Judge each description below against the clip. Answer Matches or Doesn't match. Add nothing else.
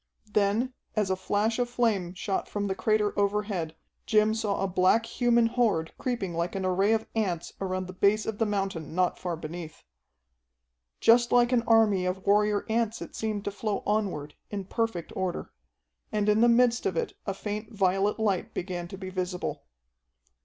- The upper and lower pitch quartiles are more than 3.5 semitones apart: Doesn't match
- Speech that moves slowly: Doesn't match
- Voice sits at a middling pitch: Doesn't match